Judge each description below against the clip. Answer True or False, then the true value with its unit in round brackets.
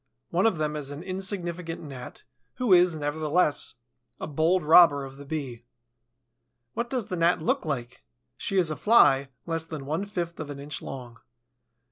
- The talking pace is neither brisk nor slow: True (170 wpm)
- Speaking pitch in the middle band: True (160 Hz)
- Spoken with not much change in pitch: False (4.0 semitones)